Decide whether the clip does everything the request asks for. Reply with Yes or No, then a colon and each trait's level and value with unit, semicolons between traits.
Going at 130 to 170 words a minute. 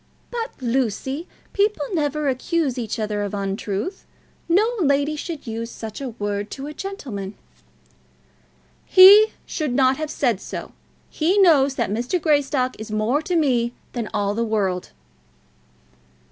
Yes: average, 140 wpm